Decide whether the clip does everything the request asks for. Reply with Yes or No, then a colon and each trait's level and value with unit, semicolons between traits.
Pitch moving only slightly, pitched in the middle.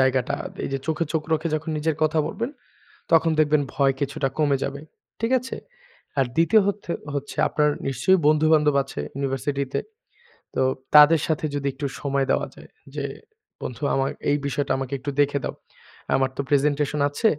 Yes: narrow, 2.3 semitones; medium, 145 Hz